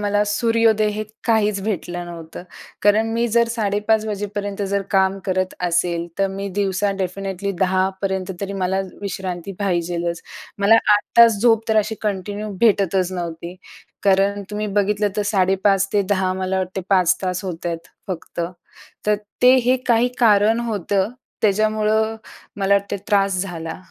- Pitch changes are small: Yes, narrow, 2.2 semitones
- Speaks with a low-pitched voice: No, high, 200 Hz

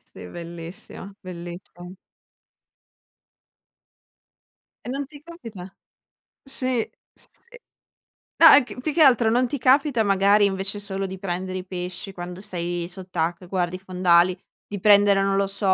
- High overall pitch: Yes, high, 195 Hz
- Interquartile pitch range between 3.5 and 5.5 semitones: Yes, average, 3.8 semitones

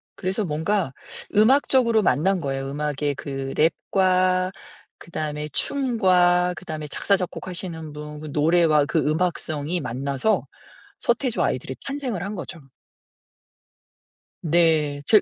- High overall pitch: No, medium, 170 Hz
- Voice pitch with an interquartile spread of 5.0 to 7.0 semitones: No, average, 4.2 semitones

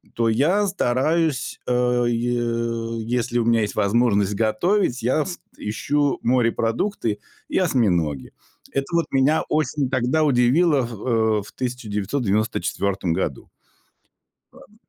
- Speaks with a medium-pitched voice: No, low, 120 Hz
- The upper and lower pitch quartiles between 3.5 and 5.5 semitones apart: Yes, average, 3.8 semitones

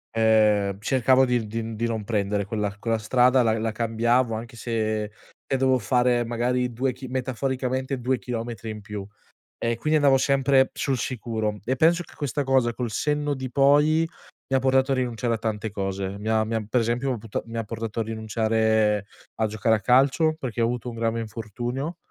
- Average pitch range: Yes, average, 3.0 semitones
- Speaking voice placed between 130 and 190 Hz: No, low, 115 Hz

